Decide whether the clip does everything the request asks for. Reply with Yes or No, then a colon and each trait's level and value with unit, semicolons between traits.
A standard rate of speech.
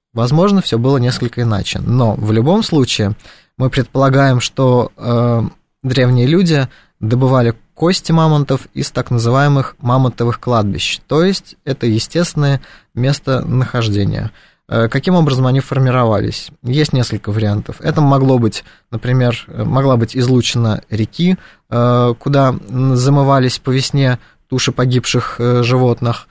Yes: average, 120 wpm